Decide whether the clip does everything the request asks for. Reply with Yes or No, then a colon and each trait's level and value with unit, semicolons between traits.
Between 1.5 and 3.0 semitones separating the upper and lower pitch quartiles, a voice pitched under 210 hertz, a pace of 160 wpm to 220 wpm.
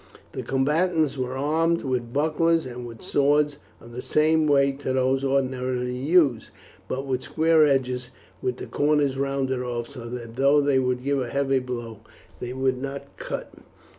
Yes: narrow, 2.5 semitones; low, 135 Hz; average, 165 wpm